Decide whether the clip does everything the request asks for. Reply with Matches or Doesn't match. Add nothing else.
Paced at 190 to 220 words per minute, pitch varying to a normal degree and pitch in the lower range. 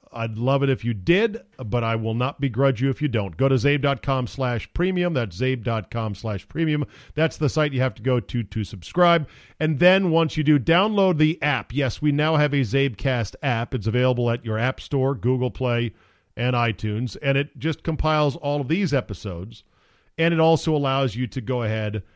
Matches